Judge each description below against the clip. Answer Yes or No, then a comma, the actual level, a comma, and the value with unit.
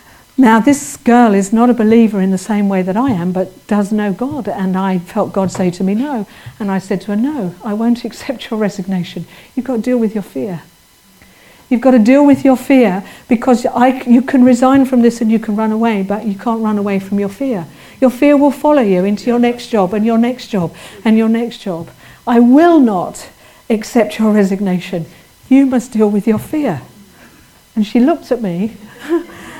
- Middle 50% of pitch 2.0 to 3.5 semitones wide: No, average, 4.0 semitones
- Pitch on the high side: Yes, high, 225 Hz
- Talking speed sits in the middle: No, fast, 215 wpm